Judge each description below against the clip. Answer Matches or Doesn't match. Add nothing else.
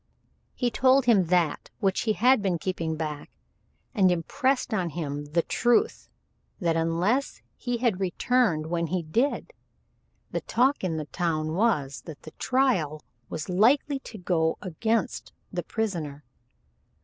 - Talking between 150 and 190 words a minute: Doesn't match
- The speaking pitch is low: Doesn't match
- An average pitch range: Doesn't match